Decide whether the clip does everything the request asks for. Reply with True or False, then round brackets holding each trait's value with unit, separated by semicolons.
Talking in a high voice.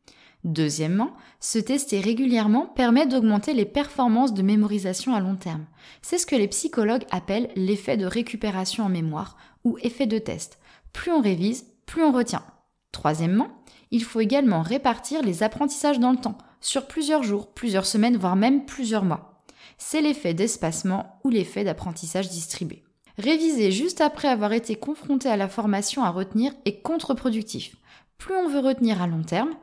True (225 Hz)